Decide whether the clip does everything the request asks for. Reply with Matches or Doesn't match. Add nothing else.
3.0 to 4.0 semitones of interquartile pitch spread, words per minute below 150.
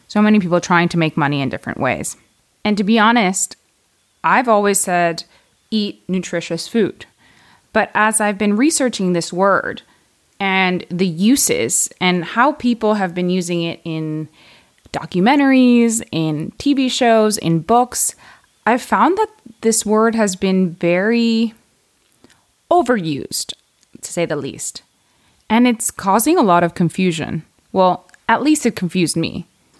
Doesn't match